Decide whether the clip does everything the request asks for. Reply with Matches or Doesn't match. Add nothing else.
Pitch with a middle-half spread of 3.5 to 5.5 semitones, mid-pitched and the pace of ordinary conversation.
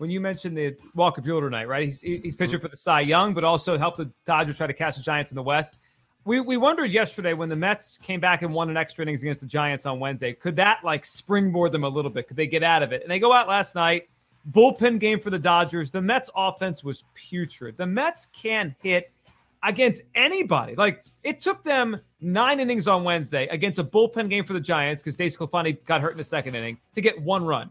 Doesn't match